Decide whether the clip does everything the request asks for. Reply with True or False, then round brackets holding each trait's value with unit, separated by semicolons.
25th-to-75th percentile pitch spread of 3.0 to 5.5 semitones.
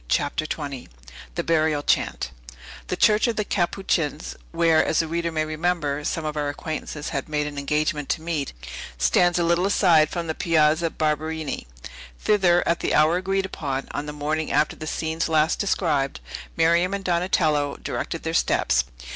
False (2.5 semitones)